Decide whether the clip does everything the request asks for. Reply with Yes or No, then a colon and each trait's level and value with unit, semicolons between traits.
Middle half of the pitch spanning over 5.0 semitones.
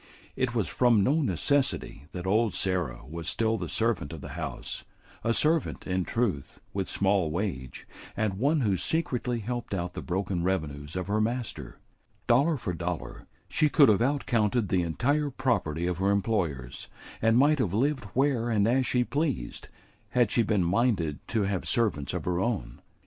Yes: wide, 5.5 semitones